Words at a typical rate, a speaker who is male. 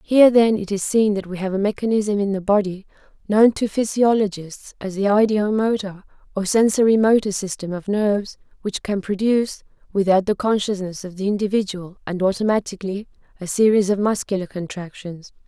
No: average, 165 wpm; female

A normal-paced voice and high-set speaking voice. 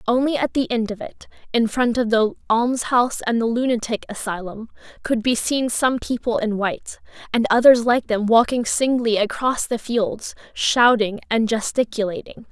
Yes: average, 165 wpm; high, 230 Hz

